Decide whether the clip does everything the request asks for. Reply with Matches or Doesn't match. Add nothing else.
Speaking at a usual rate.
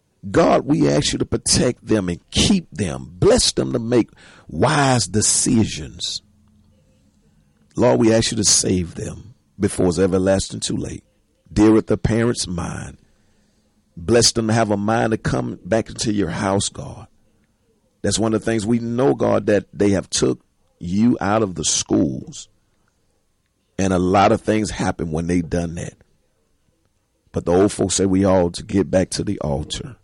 Matches